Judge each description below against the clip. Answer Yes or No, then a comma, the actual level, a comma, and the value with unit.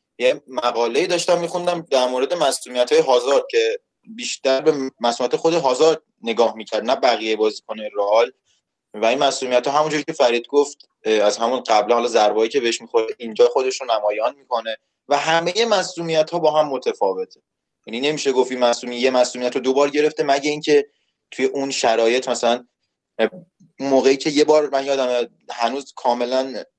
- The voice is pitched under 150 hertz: Yes, low, 135 Hz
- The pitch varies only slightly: No, average, 5.0 semitones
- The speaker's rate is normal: No, fast, 160 wpm